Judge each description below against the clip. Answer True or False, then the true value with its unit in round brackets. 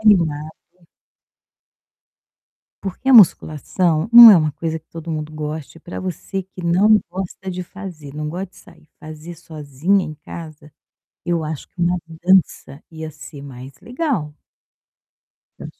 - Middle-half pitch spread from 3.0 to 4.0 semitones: True (3.5 semitones)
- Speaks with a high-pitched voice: False (165 Hz)